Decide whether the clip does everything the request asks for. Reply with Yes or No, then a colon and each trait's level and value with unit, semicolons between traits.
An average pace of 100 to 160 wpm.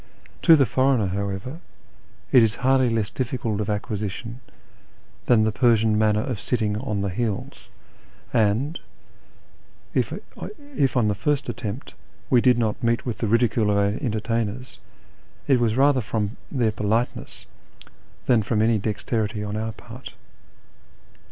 Yes: average, 140 wpm